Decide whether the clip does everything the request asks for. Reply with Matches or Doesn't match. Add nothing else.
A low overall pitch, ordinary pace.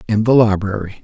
Matches